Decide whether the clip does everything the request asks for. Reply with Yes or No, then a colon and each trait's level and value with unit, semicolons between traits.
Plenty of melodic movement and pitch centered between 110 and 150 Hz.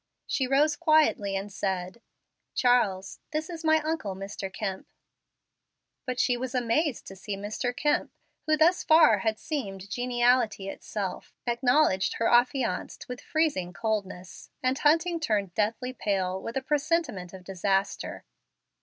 No: wide, 7.0 semitones; high, 235 Hz